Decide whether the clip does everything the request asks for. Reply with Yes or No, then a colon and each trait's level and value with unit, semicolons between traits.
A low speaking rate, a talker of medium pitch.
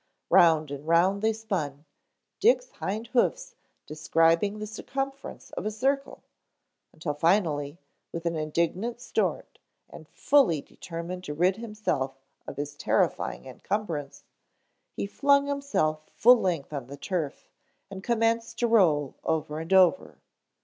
Yes: slow, 130 wpm; medium, 180 Hz